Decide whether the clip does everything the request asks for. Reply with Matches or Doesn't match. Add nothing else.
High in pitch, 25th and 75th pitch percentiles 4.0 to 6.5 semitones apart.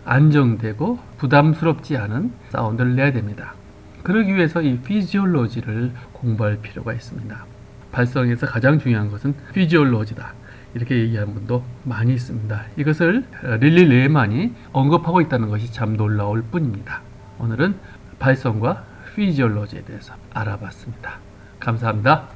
Doesn't match